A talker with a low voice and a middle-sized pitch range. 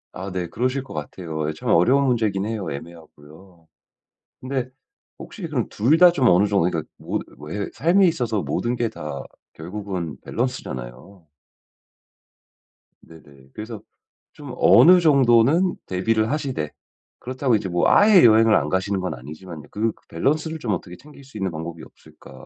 No: low, 105 Hz; wide, 7.6 semitones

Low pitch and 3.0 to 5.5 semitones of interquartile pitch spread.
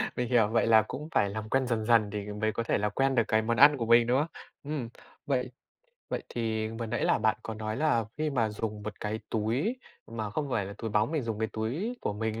No: low, 115 Hz; narrow, 2.6 semitones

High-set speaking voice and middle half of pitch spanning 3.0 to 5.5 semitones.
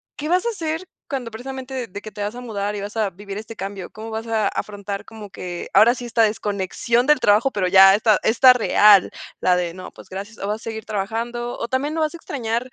Yes: high, 220 Hz; average, 3.4 semitones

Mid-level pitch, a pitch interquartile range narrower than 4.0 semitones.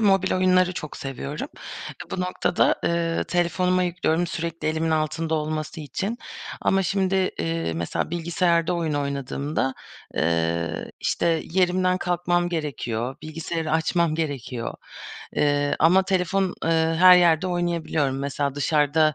Yes: medium, 165 Hz; average, 3.5 semitones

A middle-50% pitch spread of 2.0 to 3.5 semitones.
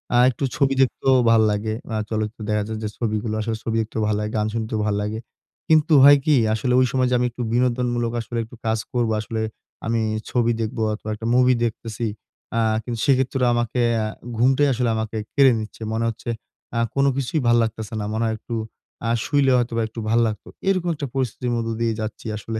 Yes: narrow, 2.4 semitones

